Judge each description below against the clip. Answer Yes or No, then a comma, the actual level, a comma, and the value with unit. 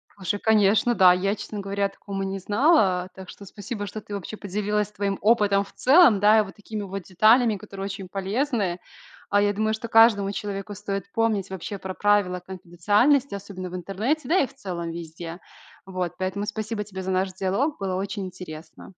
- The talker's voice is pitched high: Yes, high, 200 Hz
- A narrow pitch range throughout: Yes, narrow, 2.2 semitones